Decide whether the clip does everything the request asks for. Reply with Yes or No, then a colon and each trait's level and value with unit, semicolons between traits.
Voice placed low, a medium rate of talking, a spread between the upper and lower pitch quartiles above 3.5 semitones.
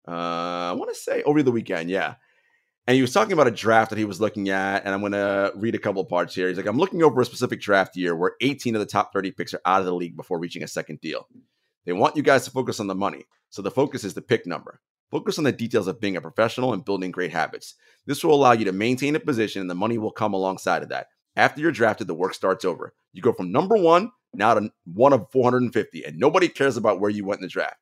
No: low, 105 Hz; fast, 270 wpm; average, 4.7 semitones